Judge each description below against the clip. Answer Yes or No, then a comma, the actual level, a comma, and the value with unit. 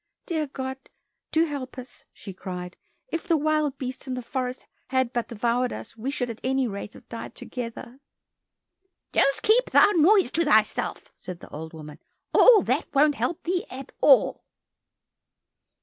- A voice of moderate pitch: No, very high, 260 Hz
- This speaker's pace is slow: No, average, 165 wpm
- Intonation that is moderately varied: Yes, average, 4.7 semitones